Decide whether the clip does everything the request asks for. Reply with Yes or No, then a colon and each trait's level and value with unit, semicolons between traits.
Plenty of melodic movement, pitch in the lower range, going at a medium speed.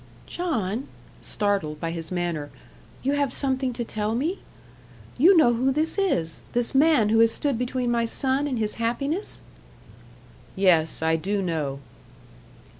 No: wide, 6.8 semitones; high, 230 Hz; average, 145 wpm